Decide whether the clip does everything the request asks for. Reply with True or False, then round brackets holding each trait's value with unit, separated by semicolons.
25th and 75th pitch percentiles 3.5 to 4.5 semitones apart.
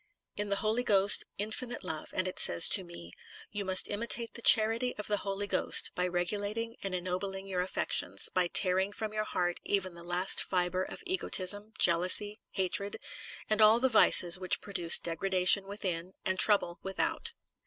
False (2.6 semitones)